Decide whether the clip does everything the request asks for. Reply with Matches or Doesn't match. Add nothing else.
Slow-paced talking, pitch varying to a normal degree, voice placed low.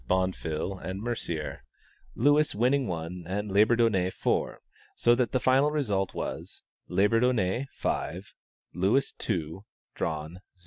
Matches